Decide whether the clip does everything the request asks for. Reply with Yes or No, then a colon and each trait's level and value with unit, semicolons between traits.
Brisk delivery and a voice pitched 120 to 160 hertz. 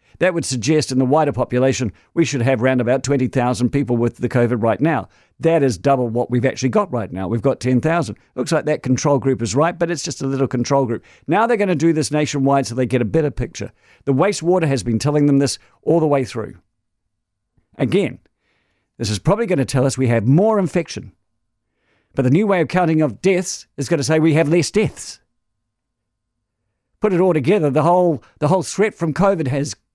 Yes: fast, 220 wpm; low, 135 Hz